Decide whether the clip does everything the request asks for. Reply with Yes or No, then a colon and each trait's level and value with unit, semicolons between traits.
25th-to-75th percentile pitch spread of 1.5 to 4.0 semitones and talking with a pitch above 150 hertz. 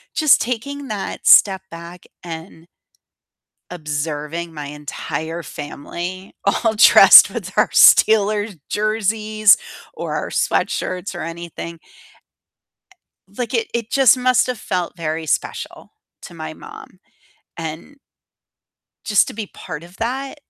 No: average, 5.1 semitones; medium, 185 Hz